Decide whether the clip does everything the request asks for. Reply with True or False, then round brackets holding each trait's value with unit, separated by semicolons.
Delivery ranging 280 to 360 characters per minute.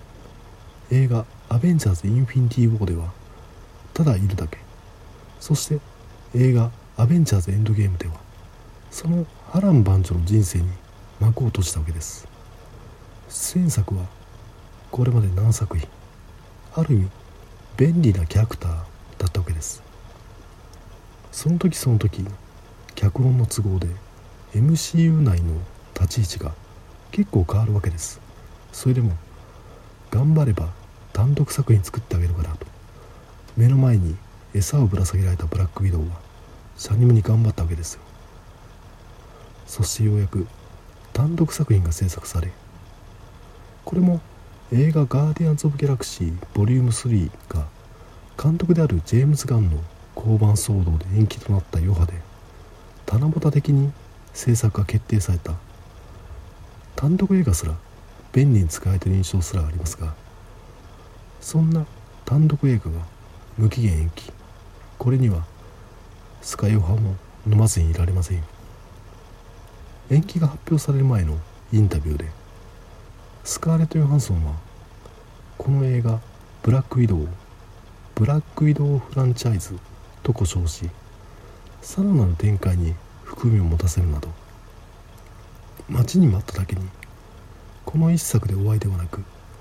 True (285 characters per minute)